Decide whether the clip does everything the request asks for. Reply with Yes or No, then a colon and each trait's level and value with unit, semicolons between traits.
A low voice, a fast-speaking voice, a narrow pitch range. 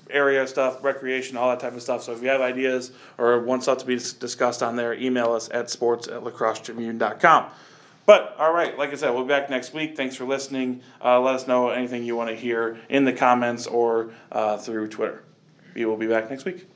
Yes: low, 125 Hz; fast, 220 wpm; narrow, 1.8 semitones